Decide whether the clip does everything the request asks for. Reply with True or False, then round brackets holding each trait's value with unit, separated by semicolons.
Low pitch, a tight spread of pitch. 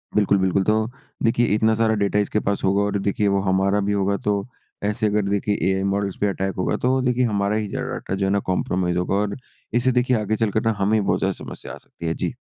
True (100 Hz; 1.9 semitones)